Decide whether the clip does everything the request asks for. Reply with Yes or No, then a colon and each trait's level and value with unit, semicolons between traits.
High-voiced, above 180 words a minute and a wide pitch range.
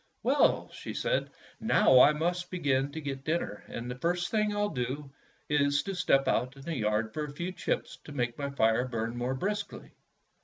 No: medium, 140 Hz; average, 200 wpm; wide, 5.7 semitones